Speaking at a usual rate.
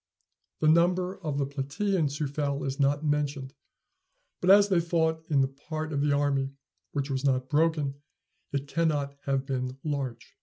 Yes: average, 165 wpm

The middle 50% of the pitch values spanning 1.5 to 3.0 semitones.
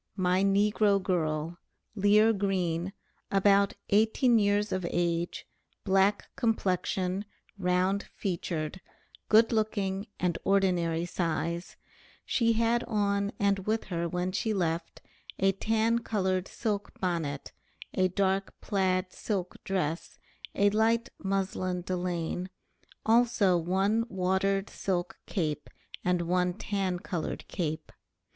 Yes: narrow, 2.4 semitones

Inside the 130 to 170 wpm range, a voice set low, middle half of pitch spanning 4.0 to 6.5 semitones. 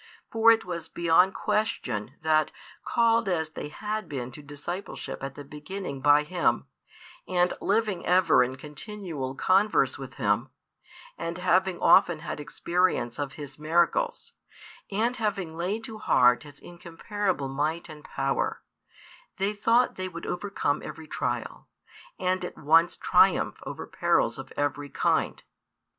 No: average, 140 wpm; medium, 170 Hz; average, 5.1 semitones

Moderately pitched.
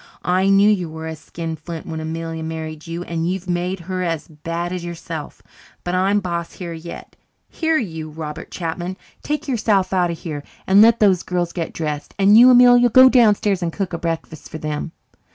Yes: medium, 175 Hz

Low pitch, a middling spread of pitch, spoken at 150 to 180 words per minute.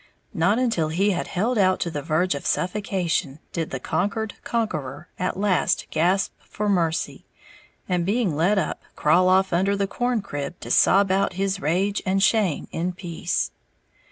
No: medium, 185 Hz; average, 3.2 semitones; average, 160 wpm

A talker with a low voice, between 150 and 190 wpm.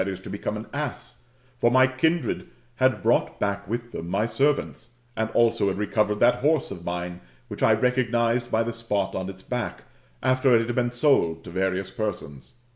Yes: low, 115 Hz; average, 185 wpm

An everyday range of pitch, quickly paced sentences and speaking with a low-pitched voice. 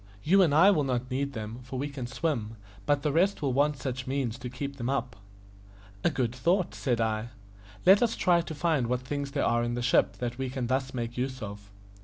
Yes: average, 3.2 semitones; fast, 235 wpm; low, 130 Hz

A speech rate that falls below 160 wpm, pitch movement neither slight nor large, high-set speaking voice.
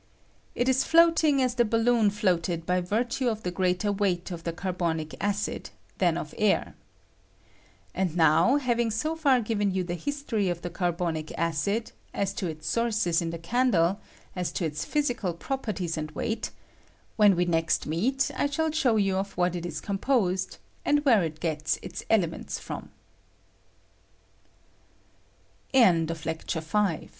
No: average, 145 wpm; wide, 5.7 semitones; high, 195 Hz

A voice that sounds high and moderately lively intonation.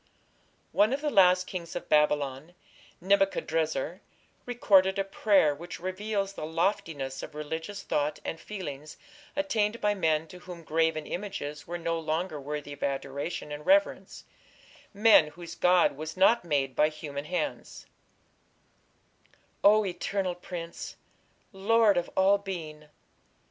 No: medium, 175 Hz; average, 4.5 semitones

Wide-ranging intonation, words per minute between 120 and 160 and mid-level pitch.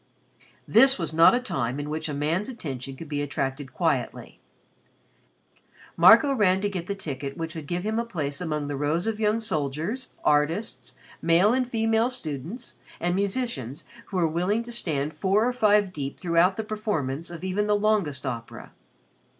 No: wide, 6.5 semitones; average, 175 wpm; medium, 175 Hz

